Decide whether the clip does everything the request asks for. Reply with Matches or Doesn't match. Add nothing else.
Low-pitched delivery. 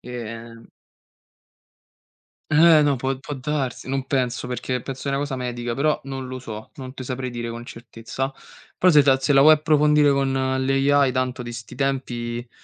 Matches